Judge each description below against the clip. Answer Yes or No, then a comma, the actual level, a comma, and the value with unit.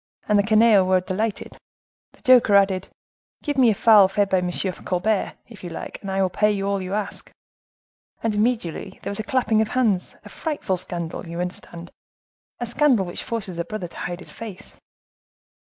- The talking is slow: No, average, 190 wpm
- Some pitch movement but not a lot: Yes, average, 3.2 semitones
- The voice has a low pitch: No, high, 200 Hz